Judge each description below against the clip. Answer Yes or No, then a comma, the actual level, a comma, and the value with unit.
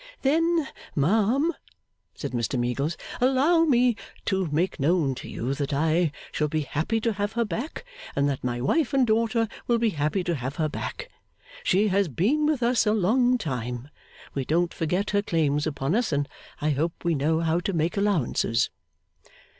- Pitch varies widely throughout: Yes, wide, 8.0 semitones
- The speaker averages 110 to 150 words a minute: No, average, 180 wpm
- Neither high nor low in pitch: Yes, medium, 175 Hz